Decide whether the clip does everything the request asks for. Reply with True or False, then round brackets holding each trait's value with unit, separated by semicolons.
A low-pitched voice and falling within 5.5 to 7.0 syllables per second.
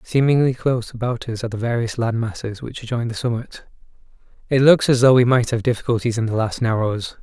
True (120 Hz; 6.0 syllables/s)